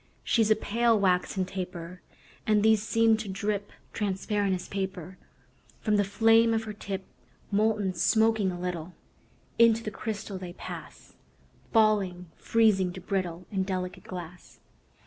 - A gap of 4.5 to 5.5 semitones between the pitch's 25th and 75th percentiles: No, average, 3.0 semitones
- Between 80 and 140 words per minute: Yes, slow, 135 wpm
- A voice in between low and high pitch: No, high, 200 Hz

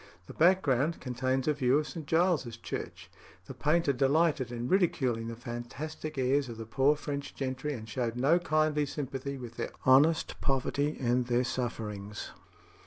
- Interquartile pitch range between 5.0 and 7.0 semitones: No, average, 3.7 semitones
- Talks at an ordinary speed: Yes, average, 160 wpm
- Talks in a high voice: No, low, 135 Hz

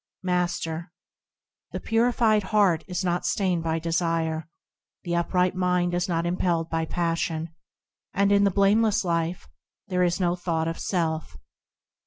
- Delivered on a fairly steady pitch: Yes, narrow, 2.1 semitones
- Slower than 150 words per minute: Yes, average, 140 wpm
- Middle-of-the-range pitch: Yes, medium, 175 Hz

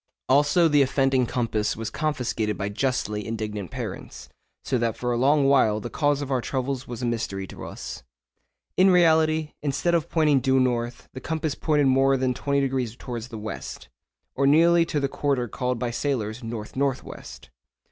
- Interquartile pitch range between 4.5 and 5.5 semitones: No, average, 3.7 semitones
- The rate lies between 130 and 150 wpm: No, average, 180 wpm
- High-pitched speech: No, low, 130 Hz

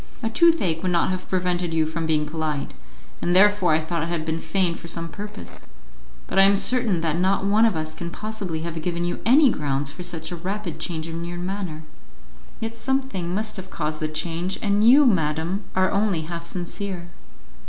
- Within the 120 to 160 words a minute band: No, average, 200 wpm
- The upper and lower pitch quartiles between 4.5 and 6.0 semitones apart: No, average, 3.7 semitones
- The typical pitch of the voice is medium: Yes, medium, 175 Hz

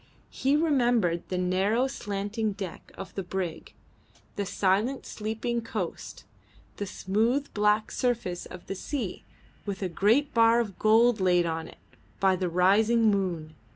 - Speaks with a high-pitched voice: Yes, high, 205 Hz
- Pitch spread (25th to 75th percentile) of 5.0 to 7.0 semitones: No, average, 3.8 semitones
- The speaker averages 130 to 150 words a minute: Yes, average, 145 wpm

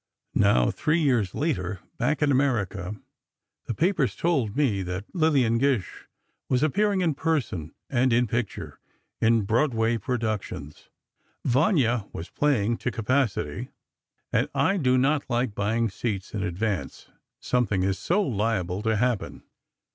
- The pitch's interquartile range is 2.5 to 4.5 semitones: No, wide, 5.5 semitones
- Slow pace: Yes, slow, 130 wpm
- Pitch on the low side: Yes, low, 120 Hz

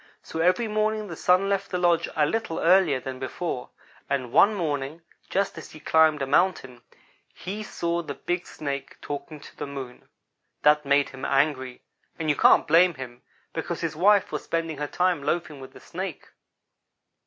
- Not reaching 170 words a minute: No, average, 175 wpm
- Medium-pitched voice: Yes, medium, 160 Hz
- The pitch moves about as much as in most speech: Yes, average, 4.4 semitones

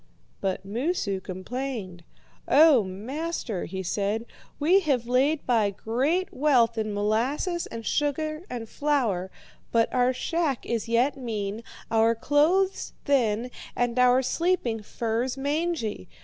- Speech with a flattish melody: No, average, 5.1 semitones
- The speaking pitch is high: Yes, high, 245 Hz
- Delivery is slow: Yes, slow, 120 wpm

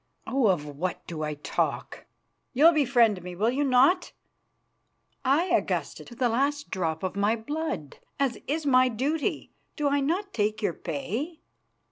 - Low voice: No, very high, 250 Hz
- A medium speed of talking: Yes, average, 155 wpm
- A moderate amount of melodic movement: No, wide, 7.5 semitones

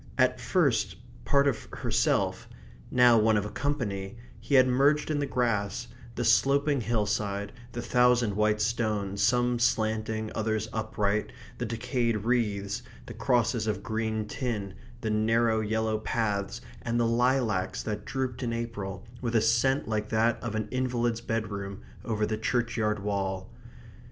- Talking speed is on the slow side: No, average, 145 wpm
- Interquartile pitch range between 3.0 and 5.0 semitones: No, narrow, 2.4 semitones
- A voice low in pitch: Yes, low, 110 Hz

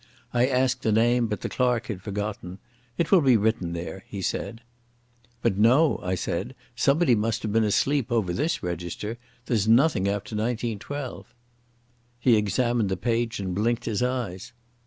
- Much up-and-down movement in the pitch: No, average, 3.5 semitones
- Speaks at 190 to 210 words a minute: No, average, 160 wpm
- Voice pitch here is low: Yes, low, 115 Hz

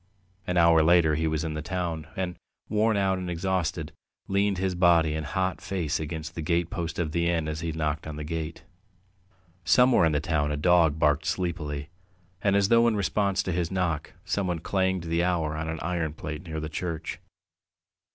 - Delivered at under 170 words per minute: No, average, 190 wpm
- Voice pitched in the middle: No, very low, 85 Hz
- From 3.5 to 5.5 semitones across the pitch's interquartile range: No, average, 2.9 semitones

